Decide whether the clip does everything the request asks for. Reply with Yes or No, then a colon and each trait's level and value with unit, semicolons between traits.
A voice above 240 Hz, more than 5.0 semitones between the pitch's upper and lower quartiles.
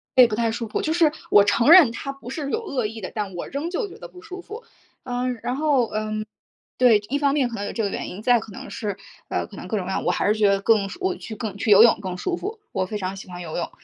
No: high, 230 Hz; wide, 5.5 semitones